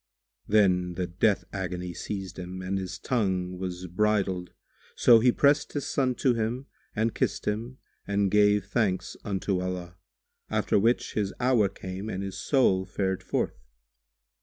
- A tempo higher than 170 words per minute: No, average, 150 wpm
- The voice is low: Yes, low, 100 Hz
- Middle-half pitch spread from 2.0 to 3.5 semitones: Yes, average, 3.1 semitones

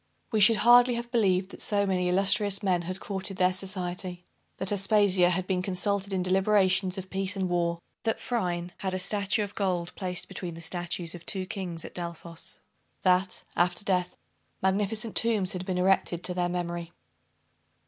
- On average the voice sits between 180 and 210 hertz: Yes, medium, 185 Hz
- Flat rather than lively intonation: Yes, narrow, 2.0 semitones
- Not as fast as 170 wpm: No, average, 175 wpm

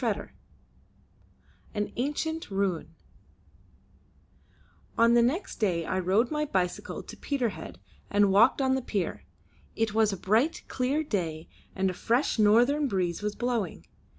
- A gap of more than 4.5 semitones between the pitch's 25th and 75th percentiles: Yes, average, 5.2 semitones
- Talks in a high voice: Yes, high, 220 Hz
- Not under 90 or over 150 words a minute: Yes, average, 145 wpm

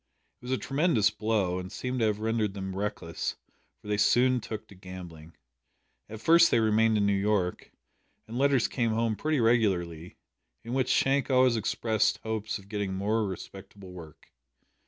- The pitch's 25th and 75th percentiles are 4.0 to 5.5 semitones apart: No, average, 3.3 semitones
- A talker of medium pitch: No, low, 110 Hz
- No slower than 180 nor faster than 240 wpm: No, average, 170 wpm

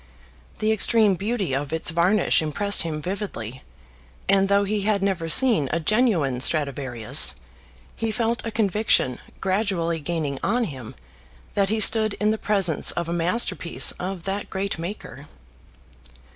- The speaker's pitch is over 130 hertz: Yes, high, 190 Hz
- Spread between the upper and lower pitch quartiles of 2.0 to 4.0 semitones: No, average, 5.0 semitones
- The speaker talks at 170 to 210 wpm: No, average, 145 wpm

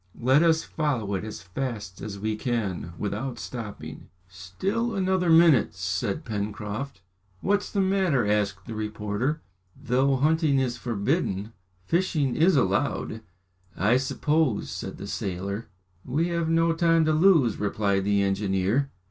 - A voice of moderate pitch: No, low, 120 Hz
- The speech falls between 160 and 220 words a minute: No, slow, 135 wpm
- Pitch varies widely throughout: Yes, wide, 7.9 semitones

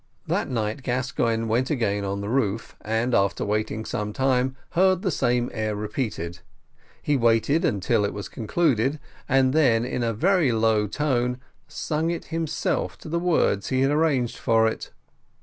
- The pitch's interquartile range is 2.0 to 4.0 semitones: No, average, 4.7 semitones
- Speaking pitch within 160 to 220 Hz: No, low, 120 Hz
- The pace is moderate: Yes, average, 165 wpm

